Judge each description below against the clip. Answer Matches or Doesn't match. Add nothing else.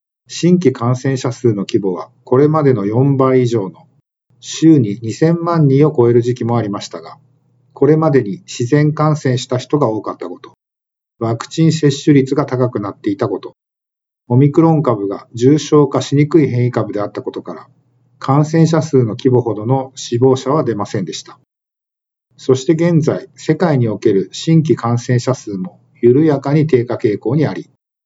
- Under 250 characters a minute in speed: Doesn't match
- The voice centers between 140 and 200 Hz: Doesn't match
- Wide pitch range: Doesn't match